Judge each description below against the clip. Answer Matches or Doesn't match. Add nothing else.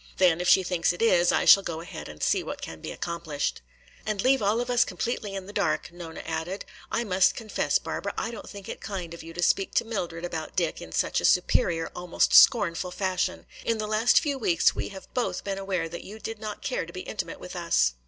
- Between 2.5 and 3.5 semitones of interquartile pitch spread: Doesn't match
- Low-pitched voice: Doesn't match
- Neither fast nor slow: Doesn't match